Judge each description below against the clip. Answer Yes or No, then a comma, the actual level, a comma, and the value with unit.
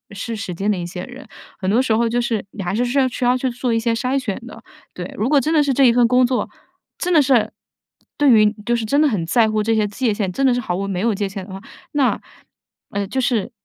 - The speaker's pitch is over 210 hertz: Yes, high, 230 Hz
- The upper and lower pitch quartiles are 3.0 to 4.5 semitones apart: Yes, average, 3.8 semitones